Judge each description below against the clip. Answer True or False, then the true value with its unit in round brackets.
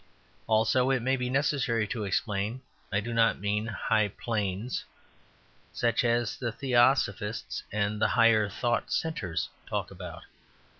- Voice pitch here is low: True (115 Hz)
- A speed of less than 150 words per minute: True (135 wpm)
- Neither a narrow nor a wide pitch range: True (3.0 semitones)